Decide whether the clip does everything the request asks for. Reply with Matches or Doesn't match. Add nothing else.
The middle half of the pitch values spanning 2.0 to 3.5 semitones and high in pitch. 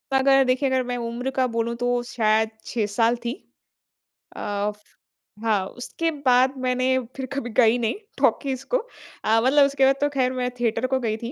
Matches